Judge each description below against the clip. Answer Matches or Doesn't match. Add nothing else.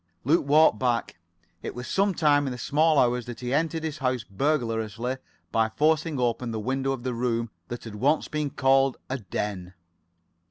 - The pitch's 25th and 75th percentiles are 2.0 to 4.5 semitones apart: Matches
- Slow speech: Doesn't match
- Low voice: Matches